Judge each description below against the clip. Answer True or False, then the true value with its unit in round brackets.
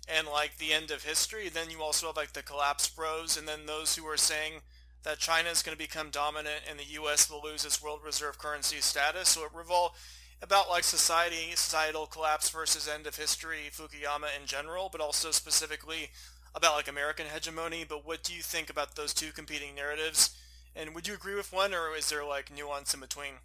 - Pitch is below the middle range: False (155 Hz)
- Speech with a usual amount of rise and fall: False (1.5 semitones)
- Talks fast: True (210 wpm)